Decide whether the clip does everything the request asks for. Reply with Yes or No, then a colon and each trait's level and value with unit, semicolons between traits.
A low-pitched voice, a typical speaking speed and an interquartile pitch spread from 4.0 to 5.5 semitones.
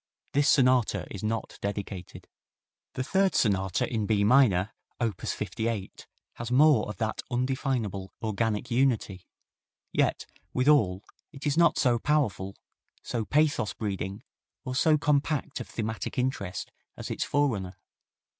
No: low, 115 Hz; slow, 125 wpm; average, 5.0 semitones